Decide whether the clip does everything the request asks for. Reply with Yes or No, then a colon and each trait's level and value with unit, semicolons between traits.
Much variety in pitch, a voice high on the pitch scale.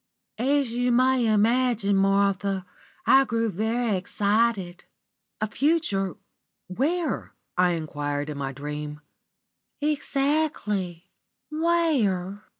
Yes: wide, 6.1 semitones; high, 210 Hz